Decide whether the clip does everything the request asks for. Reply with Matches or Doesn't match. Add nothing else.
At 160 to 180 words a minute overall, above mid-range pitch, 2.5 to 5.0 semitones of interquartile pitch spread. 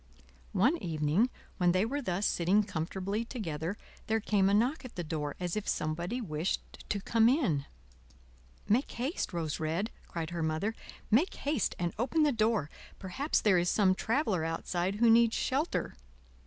Doesn't match